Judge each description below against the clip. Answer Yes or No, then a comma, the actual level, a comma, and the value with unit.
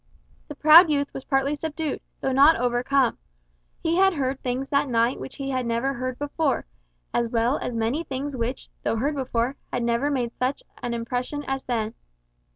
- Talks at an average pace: Yes, average, 180 wpm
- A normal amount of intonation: Yes, average, 3.0 semitones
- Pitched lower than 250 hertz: No, very high, 265 Hz